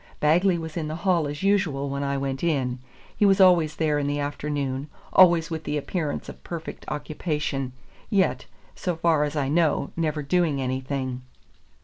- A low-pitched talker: No, medium, 150 Hz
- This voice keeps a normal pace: Yes, average, 170 wpm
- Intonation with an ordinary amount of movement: Yes, average, 3.3 semitones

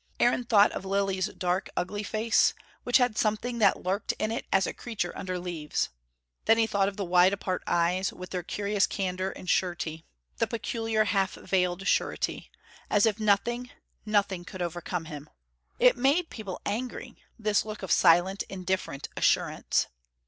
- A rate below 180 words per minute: Yes, average, 165 wpm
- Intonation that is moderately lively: Yes, average, 3.0 semitones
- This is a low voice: No, high, 195 Hz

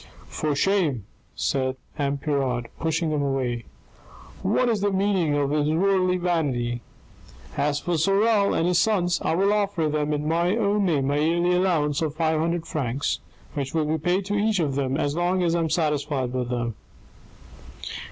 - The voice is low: No, medium, 160 Hz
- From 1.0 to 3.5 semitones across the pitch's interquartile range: No, average, 4.2 semitones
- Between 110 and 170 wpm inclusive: No, average, 180 wpm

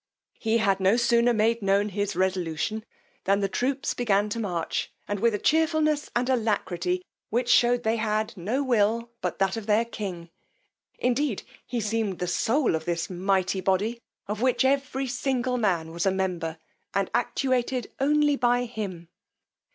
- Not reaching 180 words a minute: Yes, average, 160 wpm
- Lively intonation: No, average, 4.3 semitones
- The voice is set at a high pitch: Yes, high, 220 Hz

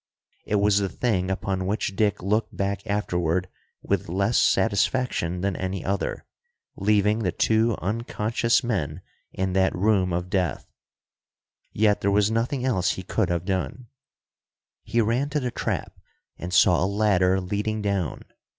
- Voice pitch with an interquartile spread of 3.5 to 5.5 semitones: No, average, 2.9 semitones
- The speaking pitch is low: Yes, low, 100 Hz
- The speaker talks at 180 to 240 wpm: No, average, 150 wpm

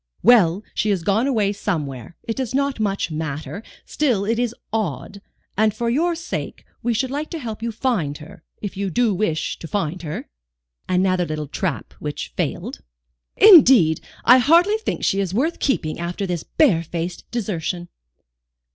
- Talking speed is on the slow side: No, average, 165 wpm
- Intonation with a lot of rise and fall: Yes, wide, 6.2 semitones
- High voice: Yes, high, 205 Hz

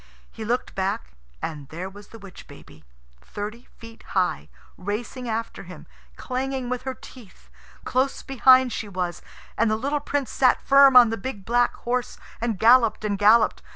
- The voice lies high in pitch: Yes, high, 230 Hz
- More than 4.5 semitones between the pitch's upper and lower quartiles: No, average, 4.0 semitones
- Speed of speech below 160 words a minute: No, average, 165 wpm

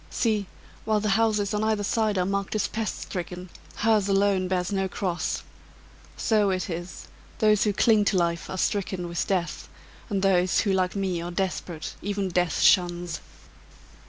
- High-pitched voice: Yes, high, 195 Hz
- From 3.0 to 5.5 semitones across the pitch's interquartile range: No, narrow, 2.6 semitones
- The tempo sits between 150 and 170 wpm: Yes, average, 165 wpm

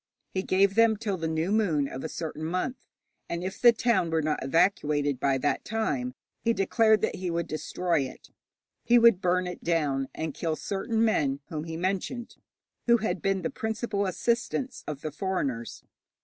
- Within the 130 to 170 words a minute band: No, average, 180 wpm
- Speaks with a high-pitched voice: No, medium, 180 Hz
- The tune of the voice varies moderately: No, wide, 6.0 semitones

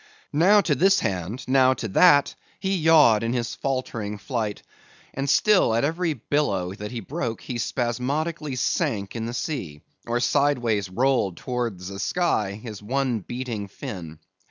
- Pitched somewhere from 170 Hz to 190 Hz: No, low, 120 Hz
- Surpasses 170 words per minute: No, average, 155 wpm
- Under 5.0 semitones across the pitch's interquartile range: No, wide, 5.5 semitones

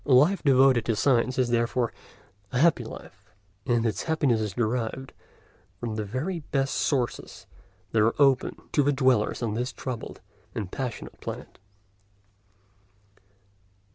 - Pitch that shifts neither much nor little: Yes, average, 3.0 semitones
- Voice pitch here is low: Yes, low, 125 Hz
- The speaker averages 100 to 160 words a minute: Yes, slow, 135 wpm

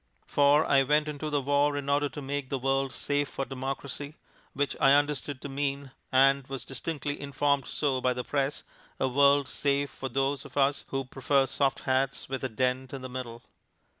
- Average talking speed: Yes, average, 195 wpm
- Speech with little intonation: Yes, narrow, 1.4 semitones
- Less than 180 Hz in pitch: Yes, medium, 140 Hz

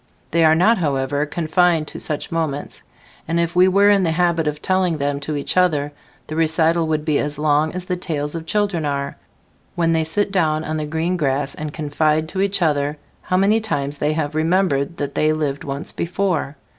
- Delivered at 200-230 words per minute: Yes, fast, 205 wpm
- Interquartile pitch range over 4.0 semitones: No, average, 3.0 semitones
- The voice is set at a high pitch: No, medium, 160 Hz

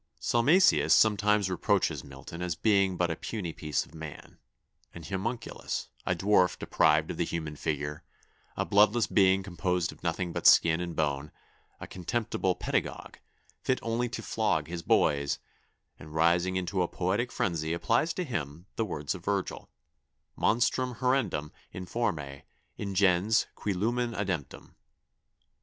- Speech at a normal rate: Yes, average, 145 wpm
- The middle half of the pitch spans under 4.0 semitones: No, average, 4.8 semitones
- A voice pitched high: No, very low, 90 Hz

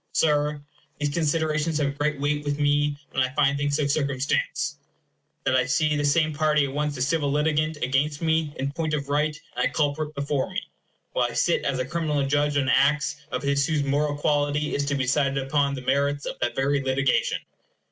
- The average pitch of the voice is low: No, medium, 145 Hz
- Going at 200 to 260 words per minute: Yes, fast, 205 wpm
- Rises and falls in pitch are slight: Yes, narrow, 1.4 semitones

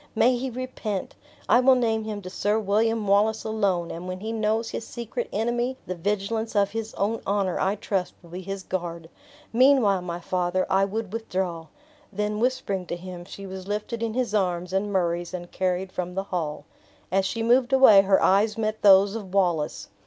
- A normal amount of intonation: Yes, average, 3.3 semitones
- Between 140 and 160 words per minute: No, average, 190 wpm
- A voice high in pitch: Yes, high, 200 Hz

